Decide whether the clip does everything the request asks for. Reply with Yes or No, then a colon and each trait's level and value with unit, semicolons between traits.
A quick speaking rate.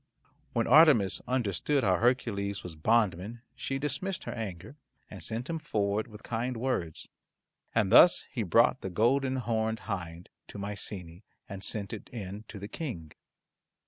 No: average, 155 wpm